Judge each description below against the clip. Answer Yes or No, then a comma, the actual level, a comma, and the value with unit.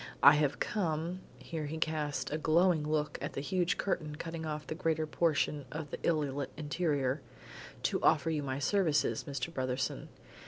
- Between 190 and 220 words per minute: No, average, 180 wpm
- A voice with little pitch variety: Yes, narrow, 2.0 semitones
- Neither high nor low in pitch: Yes, medium, 155 Hz